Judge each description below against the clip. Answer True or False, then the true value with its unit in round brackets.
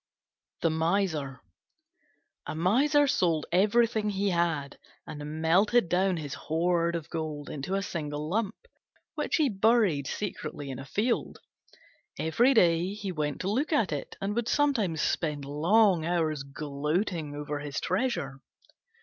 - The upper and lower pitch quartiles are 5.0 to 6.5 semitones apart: True (5.6 semitones)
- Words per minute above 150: False (140 wpm)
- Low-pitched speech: False (170 Hz)